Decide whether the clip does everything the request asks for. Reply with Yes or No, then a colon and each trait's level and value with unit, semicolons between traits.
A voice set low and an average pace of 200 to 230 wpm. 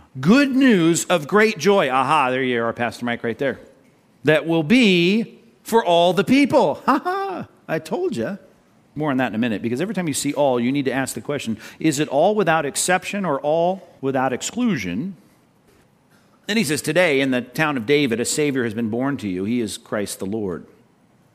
No: medium, 160 Hz; fast, 205 wpm